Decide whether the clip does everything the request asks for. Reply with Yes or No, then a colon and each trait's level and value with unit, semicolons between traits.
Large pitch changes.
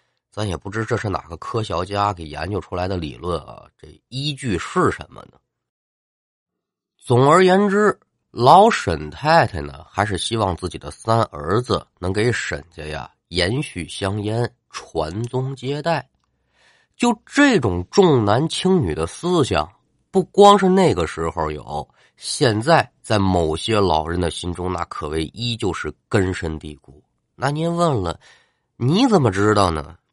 Yes: wide, 8.2 semitones